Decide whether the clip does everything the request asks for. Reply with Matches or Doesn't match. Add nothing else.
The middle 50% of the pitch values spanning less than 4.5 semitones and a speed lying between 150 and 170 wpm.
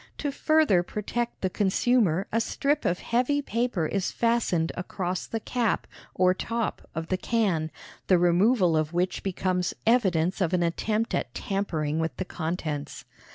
Doesn't match